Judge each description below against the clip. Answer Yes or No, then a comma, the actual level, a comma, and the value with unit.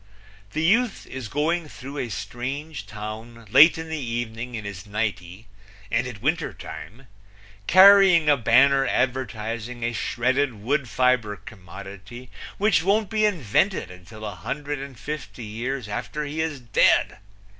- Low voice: Yes, low, 125 Hz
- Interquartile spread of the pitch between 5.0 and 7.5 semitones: Yes, wide, 5.4 semitones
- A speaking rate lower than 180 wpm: Yes, average, 145 wpm